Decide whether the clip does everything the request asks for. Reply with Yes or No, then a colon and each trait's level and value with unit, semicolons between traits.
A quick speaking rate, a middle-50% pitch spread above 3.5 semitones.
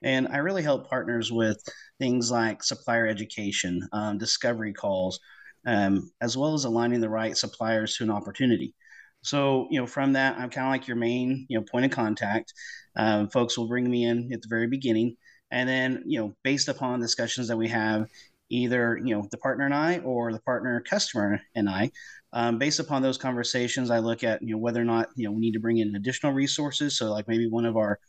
No: fast, 215 wpm; narrow, 2.5 semitones